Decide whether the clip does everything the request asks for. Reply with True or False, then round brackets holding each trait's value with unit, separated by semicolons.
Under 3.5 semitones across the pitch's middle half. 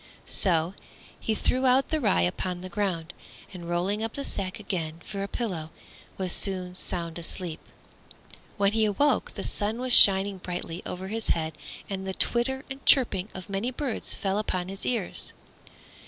False (3.8 semitones)